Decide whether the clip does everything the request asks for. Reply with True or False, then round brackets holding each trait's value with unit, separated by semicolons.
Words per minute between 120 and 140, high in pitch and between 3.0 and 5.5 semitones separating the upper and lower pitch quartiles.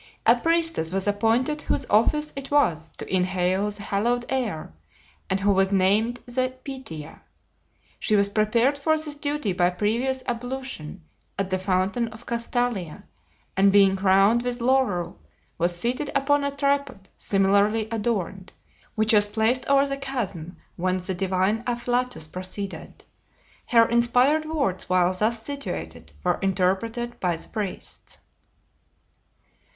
True (135 wpm; 220 Hz; 5.2 semitones)